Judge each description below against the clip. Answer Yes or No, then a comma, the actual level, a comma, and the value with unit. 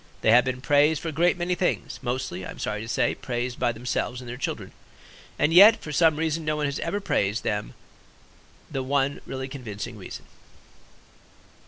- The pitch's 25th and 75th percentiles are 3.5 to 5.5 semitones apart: Yes, average, 4.7 semitones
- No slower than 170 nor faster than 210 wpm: Yes, average, 190 wpm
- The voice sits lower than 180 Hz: Yes, low, 135 Hz